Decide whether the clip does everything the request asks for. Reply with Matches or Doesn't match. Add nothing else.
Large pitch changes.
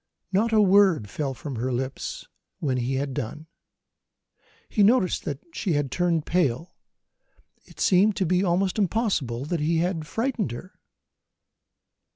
Matches